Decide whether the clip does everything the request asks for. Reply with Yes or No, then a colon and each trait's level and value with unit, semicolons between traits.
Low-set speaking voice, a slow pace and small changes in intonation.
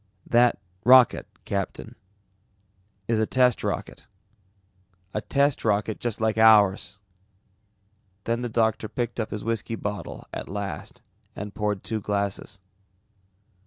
Yes: low, 110 Hz; slow, 120 wpm; narrow, 2.3 semitones